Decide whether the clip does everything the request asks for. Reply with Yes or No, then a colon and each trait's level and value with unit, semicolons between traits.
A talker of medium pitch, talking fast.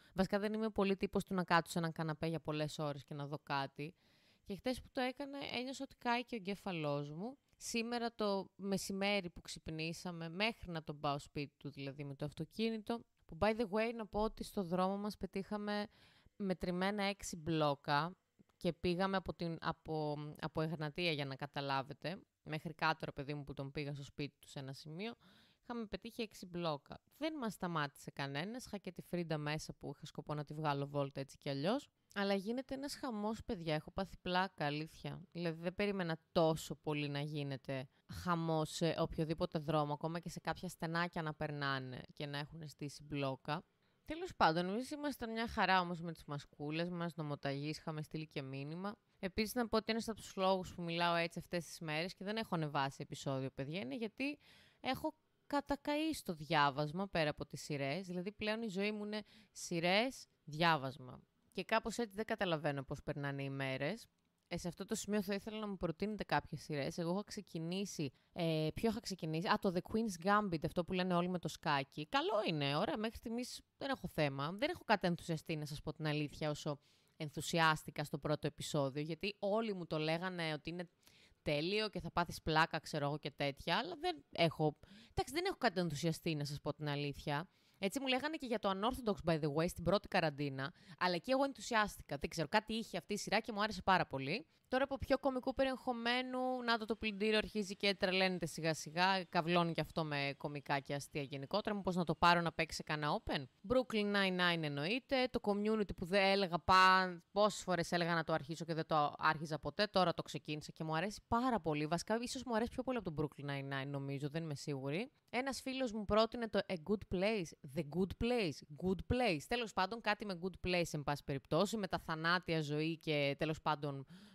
Yes: medium, 175 Hz; fast, 200 wpm